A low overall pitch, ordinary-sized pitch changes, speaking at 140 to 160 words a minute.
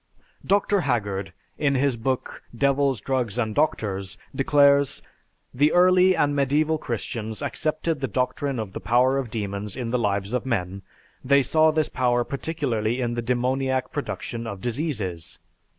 Yes: low, 125 Hz; average, 4.2 semitones; average, 150 wpm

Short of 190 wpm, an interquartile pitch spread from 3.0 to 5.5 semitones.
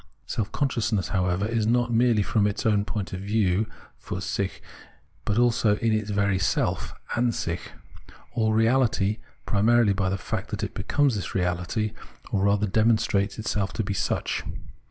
No: average, 160 wpm; narrow, 2.6 semitones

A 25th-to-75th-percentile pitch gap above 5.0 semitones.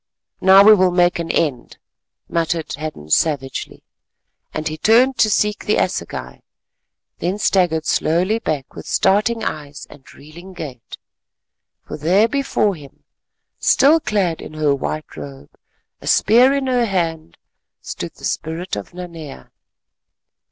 Yes: wide, 5.4 semitones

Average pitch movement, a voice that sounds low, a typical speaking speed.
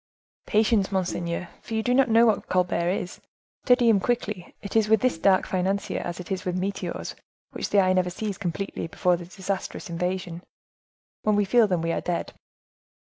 No: average, 3.1 semitones; high, 190 Hz; average, 185 wpm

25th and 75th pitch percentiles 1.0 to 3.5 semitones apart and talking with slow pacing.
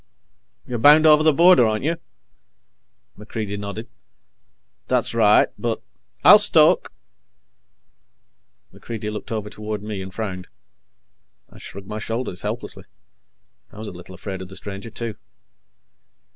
Yes: narrow, 2.6 semitones; slow, 130 wpm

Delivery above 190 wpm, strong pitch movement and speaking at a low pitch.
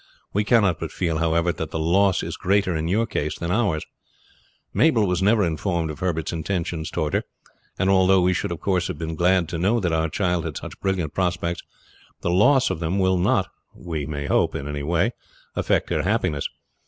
No: fast, 205 wpm; average, 3.0 semitones; very low, 90 Hz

